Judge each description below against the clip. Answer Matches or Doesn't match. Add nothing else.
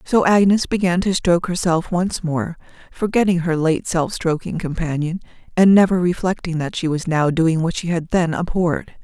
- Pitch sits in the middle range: Matches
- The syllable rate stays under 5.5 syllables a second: Matches